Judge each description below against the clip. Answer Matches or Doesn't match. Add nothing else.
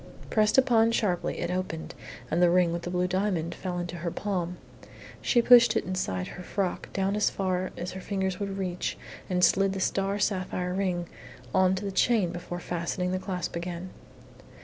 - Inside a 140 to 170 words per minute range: Doesn't match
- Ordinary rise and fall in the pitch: Doesn't match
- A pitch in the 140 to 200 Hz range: Matches